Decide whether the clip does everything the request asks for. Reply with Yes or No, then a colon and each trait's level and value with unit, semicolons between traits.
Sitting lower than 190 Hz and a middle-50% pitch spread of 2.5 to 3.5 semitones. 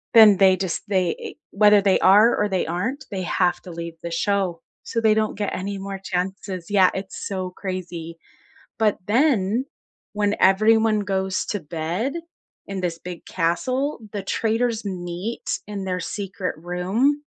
No: high, 195 Hz; average, 2.8 semitones